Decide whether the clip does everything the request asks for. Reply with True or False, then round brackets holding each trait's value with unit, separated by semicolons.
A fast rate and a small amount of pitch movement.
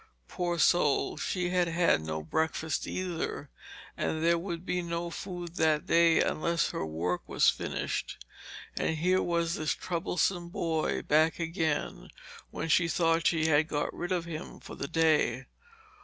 False (155 wpm; 1.9 semitones)